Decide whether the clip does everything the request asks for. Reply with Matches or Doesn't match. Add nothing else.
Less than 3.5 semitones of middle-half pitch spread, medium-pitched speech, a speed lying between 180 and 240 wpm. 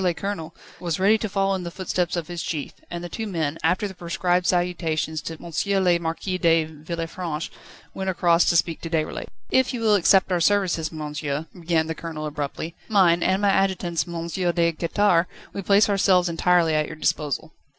Matches